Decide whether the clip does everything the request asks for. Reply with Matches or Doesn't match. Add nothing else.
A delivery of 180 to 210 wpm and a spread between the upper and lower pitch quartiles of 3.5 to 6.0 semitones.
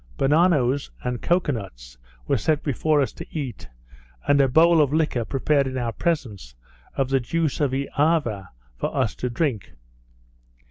Doesn't match